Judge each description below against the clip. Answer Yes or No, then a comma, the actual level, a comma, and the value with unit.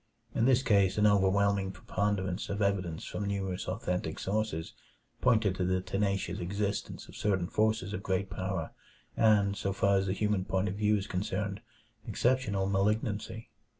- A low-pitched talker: Yes, low, 100 Hz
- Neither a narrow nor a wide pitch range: No, narrow, 1.8 semitones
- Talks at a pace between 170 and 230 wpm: No, average, 155 wpm